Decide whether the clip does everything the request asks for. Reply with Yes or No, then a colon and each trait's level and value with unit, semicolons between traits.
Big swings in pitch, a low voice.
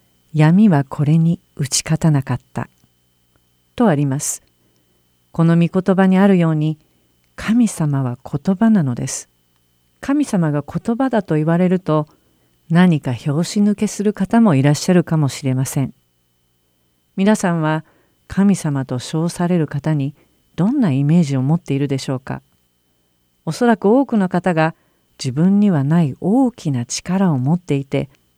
No: wide, 6.6 semitones; medium, 155 Hz